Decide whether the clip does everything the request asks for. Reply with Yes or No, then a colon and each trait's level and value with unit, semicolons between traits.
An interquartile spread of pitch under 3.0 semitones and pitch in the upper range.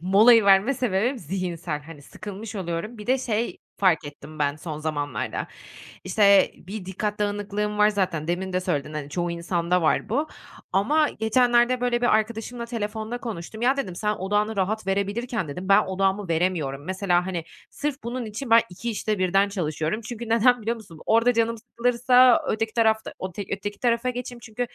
No: average, 4.4 semitones; high, 205 Hz